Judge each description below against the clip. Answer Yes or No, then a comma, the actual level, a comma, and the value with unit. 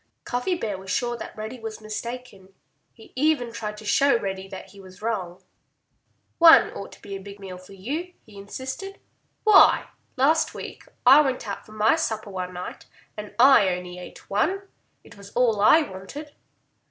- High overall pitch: Yes, high, 215 Hz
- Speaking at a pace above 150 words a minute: Yes, average, 180 wpm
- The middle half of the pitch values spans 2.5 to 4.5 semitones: No, average, 5.2 semitones